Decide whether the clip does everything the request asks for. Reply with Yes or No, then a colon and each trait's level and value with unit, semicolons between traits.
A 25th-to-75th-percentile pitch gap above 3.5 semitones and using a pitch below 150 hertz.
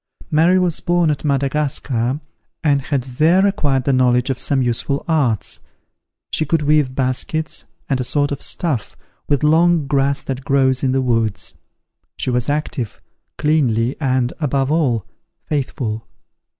No: average, 3.0 semitones; medium, 140 Hz